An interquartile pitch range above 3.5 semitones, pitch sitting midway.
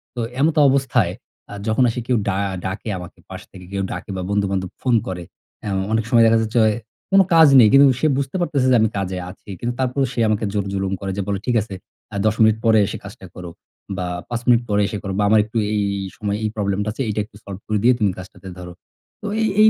No: average, 3.9 semitones; low, 110 Hz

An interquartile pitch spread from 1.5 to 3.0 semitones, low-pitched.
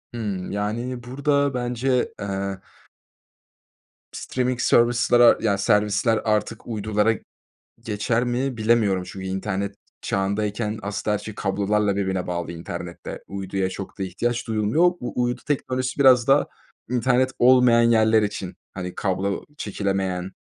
No: average, 3.8 semitones; low, 105 Hz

